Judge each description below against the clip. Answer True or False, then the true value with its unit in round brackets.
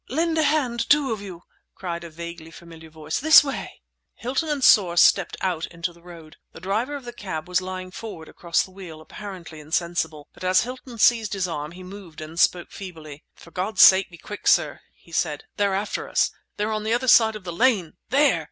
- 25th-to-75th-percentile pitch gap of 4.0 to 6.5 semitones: True (5.0 semitones)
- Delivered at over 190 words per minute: True (205 wpm)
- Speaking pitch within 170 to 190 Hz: True (185 Hz)